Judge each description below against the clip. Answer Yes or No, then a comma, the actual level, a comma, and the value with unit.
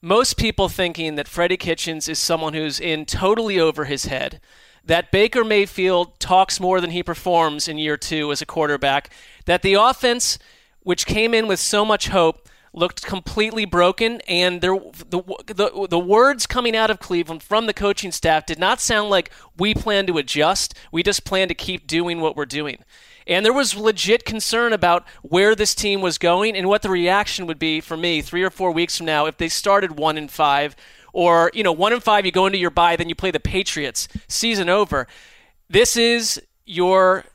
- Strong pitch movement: No, average, 3.8 semitones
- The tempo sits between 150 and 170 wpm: No, average, 200 wpm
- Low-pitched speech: No, medium, 185 Hz